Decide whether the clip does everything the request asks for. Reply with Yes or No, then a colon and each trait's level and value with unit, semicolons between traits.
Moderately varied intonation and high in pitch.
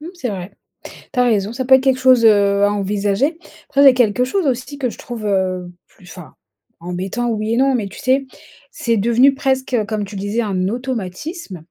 Yes: average, 4.7 semitones; high, 230 Hz